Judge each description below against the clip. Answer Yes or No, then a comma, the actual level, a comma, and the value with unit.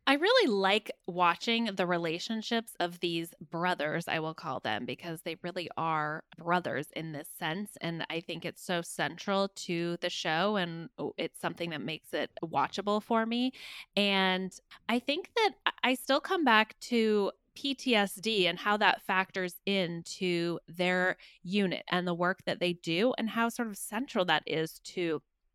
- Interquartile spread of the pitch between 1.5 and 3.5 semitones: No, average, 4.3 semitones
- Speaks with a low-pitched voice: No, medium, 185 Hz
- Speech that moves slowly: No, average, 165 wpm